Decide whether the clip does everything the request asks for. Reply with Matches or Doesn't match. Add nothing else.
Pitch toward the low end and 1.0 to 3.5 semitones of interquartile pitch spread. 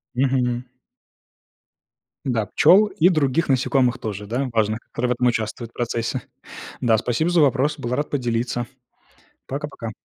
Matches